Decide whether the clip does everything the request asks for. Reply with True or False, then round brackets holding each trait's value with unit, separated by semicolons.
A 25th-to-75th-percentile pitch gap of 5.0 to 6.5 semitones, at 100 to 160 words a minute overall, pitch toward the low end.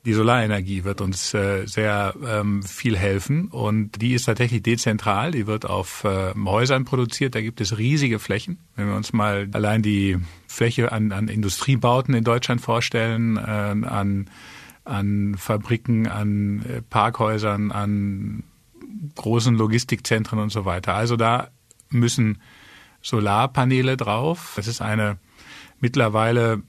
False (2.6 semitones; 125 wpm; 110 Hz)